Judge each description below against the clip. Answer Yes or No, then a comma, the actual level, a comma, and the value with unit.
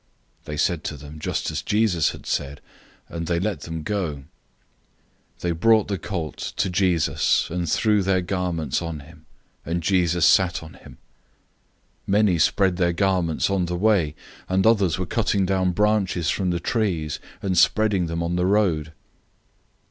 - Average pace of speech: Yes, average, 170 wpm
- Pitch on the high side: No, very low, 90 Hz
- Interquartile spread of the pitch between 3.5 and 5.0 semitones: No, average, 3.0 semitones